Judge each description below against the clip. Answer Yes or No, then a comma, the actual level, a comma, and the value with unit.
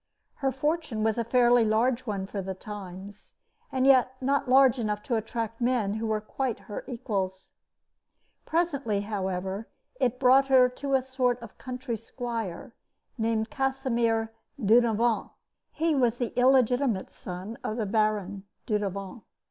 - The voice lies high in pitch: Yes, high, 230 Hz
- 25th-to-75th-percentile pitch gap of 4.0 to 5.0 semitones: No, average, 3.6 semitones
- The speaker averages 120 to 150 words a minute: Yes, average, 140 wpm